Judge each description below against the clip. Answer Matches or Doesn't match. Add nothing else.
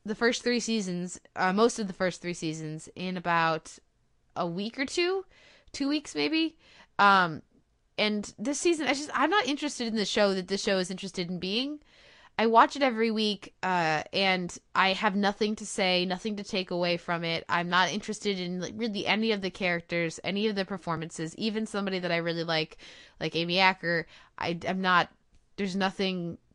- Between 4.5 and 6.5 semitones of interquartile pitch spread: Doesn't match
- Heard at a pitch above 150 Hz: Matches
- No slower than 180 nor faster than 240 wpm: Matches